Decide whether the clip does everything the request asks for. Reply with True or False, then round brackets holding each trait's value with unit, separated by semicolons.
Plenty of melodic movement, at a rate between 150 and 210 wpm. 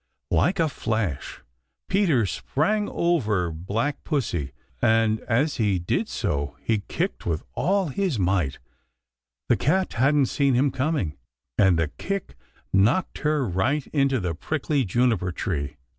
False (8.6 semitones; 135 wpm)